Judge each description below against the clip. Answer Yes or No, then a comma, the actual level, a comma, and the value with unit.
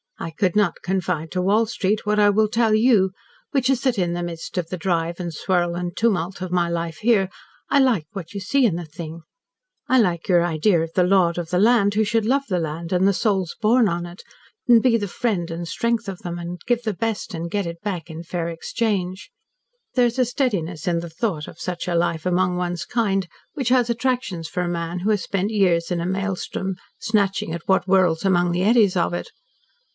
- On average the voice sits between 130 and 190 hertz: Yes, medium, 185 Hz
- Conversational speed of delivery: No, fast, 225 wpm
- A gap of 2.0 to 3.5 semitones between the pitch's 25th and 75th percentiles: No, average, 3.9 semitones